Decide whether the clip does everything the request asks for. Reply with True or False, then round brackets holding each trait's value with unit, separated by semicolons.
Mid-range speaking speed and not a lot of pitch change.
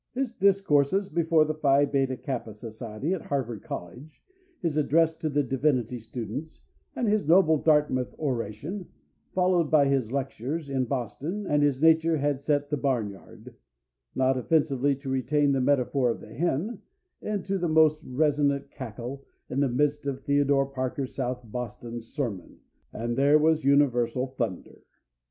False (150 wpm; 3.6 semitones)